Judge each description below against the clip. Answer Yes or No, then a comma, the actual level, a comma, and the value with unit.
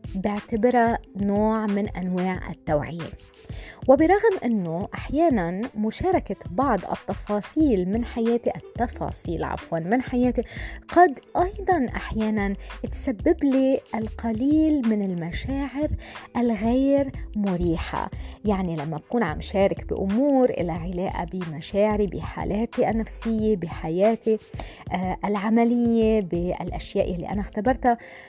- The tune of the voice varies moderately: Yes, average, 4.9 semitones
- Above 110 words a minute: No, average, 95 wpm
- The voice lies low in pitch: No, high, 220 Hz